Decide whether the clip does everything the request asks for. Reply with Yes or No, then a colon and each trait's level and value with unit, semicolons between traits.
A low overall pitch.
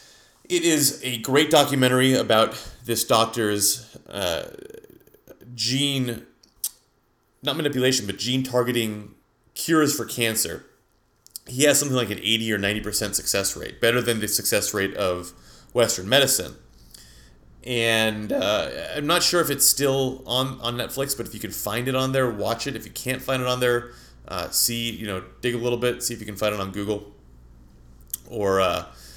Yes: low, 120 Hz